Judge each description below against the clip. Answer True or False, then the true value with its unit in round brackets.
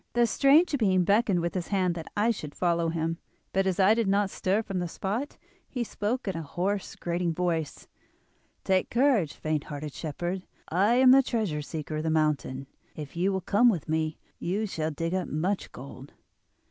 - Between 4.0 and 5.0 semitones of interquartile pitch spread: True (4.3 semitones)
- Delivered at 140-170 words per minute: False (190 wpm)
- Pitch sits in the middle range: True (180 Hz)